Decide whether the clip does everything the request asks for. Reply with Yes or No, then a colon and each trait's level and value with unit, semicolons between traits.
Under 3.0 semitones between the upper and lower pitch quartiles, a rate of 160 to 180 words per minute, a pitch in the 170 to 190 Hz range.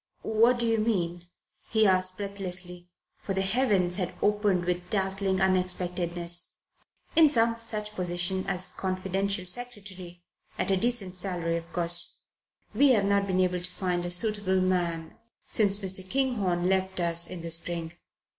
No: narrow, 2.5 semitones; average, 145 wpm; medium, 185 Hz